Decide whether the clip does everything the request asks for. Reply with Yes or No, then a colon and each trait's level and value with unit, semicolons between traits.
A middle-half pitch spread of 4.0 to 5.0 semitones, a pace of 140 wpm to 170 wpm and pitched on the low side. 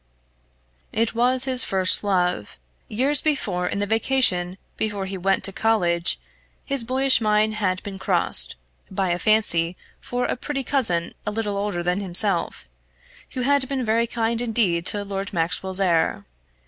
No: average, 4.4 semitones; average, 155 wpm; high, 205 Hz